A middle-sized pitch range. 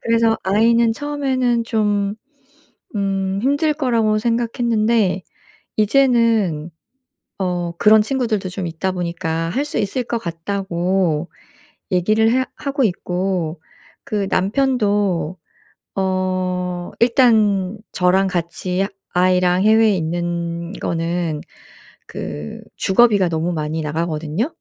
Yes: average, 4.5 semitones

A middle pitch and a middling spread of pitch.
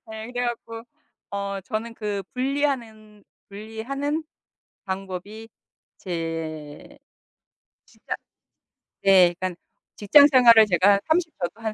No: high, 215 Hz; average, 3.9 semitones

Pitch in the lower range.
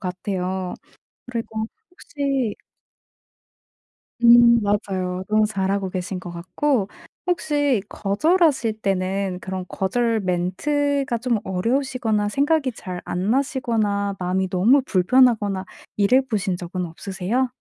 No: high, 205 Hz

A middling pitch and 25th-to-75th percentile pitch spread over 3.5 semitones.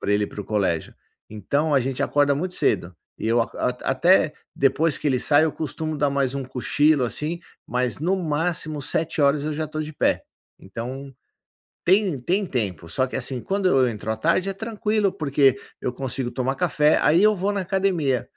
Yes: medium, 145 Hz; average, 4.6 semitones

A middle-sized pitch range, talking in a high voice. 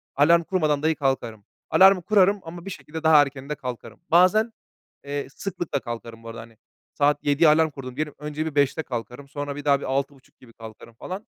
No: average, 3.6 semitones; medium, 145 Hz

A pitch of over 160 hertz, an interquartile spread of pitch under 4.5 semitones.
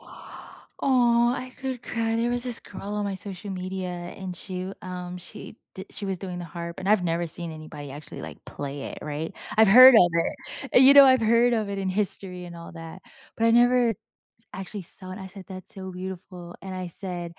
Yes: high, 190 Hz; average, 3.6 semitones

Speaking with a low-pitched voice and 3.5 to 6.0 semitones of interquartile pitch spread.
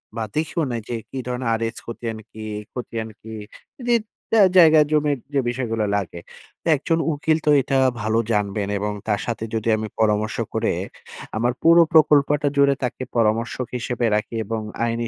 Yes: low, 120 Hz; average, 4.7 semitones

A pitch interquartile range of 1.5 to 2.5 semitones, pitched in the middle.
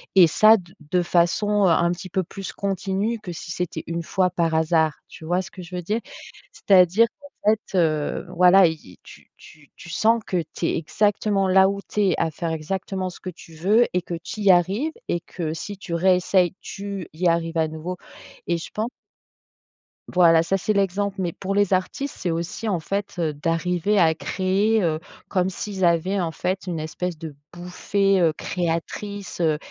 No: average, 2.9 semitones; medium, 180 Hz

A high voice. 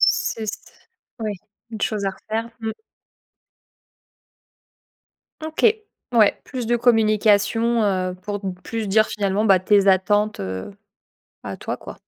Yes: high, 210 Hz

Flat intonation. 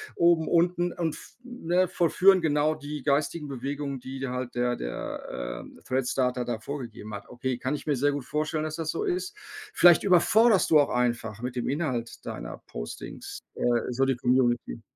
No: average, 5.1 semitones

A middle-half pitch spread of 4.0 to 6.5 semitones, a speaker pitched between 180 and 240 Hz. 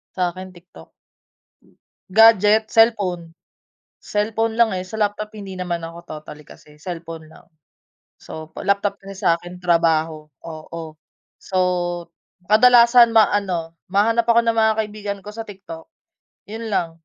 Yes: average, 4.7 semitones; high, 190 Hz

